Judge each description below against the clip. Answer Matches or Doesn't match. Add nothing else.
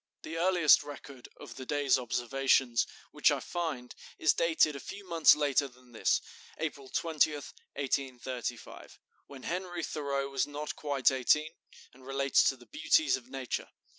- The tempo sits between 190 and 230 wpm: Doesn't match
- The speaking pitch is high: Doesn't match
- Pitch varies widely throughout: Doesn't match